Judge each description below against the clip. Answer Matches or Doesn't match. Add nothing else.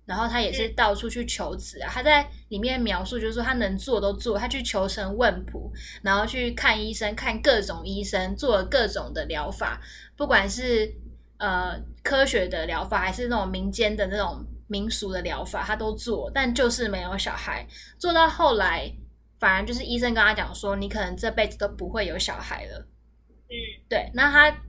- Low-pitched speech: Doesn't match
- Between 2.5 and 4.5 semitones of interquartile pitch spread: Matches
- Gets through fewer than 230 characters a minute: Doesn't match